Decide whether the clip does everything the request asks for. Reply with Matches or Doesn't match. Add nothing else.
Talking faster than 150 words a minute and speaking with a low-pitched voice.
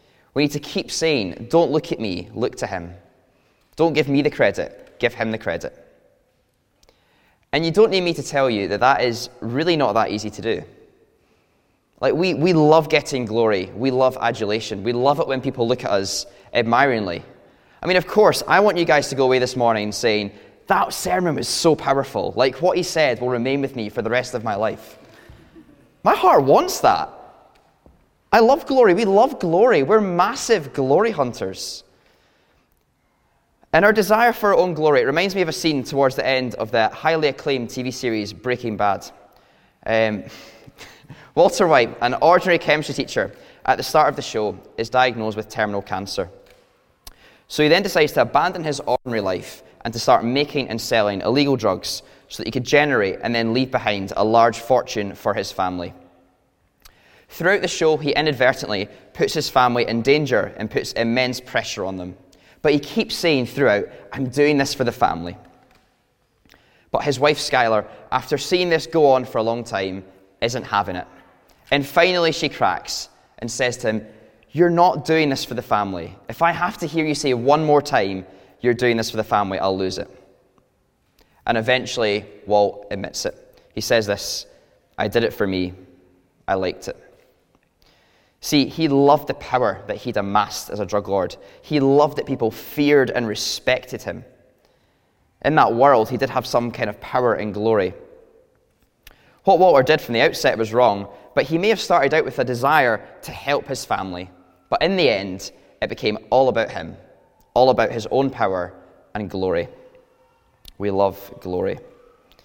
Matches